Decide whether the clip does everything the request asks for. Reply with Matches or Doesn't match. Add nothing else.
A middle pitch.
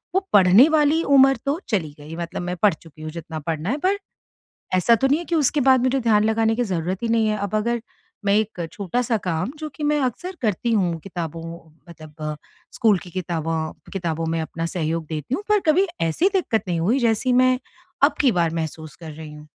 Doesn't match